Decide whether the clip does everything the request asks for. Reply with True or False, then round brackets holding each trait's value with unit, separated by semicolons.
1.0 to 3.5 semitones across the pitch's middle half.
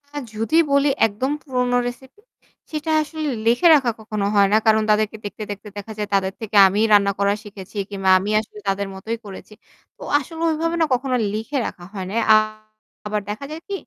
False (5.3 semitones)